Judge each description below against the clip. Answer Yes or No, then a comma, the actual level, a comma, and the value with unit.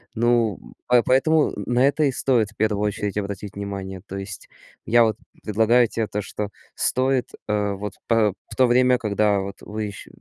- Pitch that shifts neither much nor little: Yes, average, 3.1 semitones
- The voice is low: Yes, low, 110 Hz